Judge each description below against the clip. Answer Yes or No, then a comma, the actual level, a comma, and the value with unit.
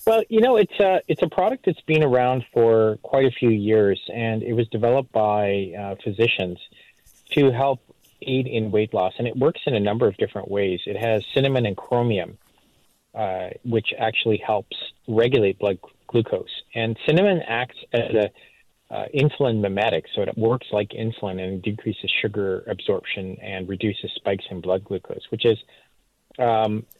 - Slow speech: No, average, 170 wpm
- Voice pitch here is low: Yes, low, 115 Hz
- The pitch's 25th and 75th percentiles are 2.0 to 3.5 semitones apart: No, average, 3.9 semitones